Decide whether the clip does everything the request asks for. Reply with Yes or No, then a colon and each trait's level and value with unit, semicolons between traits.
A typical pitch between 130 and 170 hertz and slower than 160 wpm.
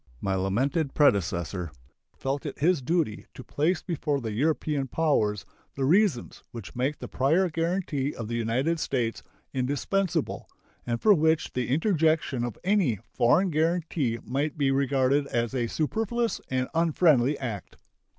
Yes: medium, 140 Hz; average, 140 wpm